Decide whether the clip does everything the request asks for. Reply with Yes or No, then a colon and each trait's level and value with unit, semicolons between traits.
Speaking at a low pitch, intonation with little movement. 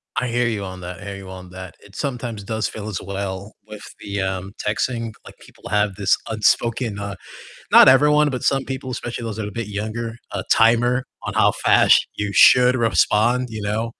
No: low, 110 Hz; average, 3.2 semitones